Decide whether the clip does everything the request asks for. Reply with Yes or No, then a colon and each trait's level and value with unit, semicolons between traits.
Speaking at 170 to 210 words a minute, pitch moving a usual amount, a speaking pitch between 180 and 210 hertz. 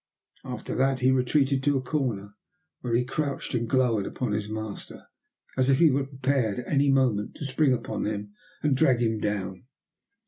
No: average, 180 wpm; average, 3.8 semitones; low, 130 Hz